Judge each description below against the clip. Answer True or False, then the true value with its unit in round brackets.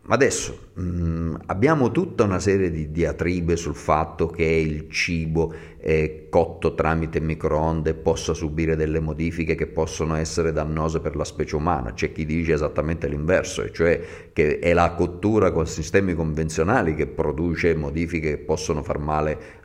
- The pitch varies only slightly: True (1.4 semitones)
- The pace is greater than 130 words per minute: True (145 wpm)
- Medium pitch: False (80 Hz)